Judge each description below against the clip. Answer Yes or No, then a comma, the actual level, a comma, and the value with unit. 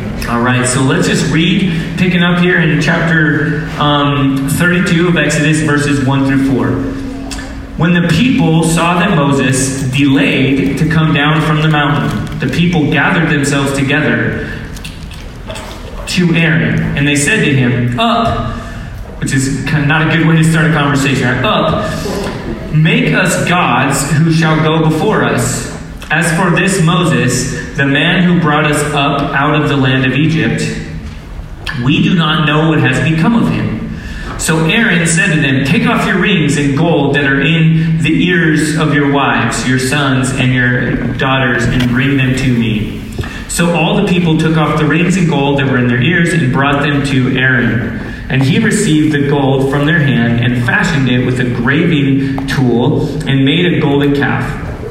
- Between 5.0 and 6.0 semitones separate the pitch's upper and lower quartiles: No, average, 3.5 semitones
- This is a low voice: No, medium, 145 Hz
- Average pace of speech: Yes, average, 175 wpm